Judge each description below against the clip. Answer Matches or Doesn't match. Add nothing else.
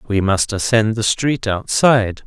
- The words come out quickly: Doesn't match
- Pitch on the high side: Doesn't match